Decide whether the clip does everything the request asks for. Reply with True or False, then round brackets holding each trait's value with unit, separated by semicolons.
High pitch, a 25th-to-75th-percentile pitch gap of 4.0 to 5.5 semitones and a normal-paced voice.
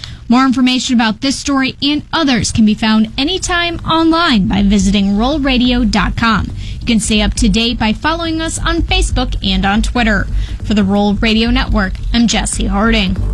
True (230 Hz; 4.3 semitones; 165 wpm)